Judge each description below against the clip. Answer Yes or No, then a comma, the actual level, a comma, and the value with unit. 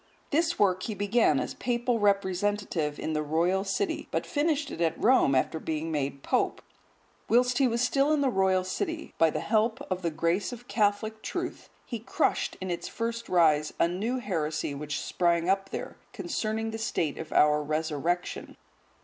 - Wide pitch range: Yes, wide, 6.3 semitones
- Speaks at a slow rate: No, average, 175 wpm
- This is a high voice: Yes, high, 195 Hz